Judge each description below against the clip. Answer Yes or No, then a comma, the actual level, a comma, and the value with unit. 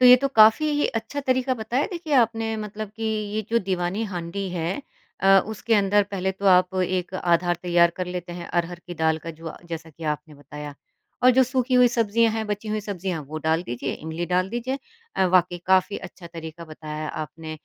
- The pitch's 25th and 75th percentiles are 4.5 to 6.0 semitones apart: Yes, average, 4.8 semitones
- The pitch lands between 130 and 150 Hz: No, medium, 185 Hz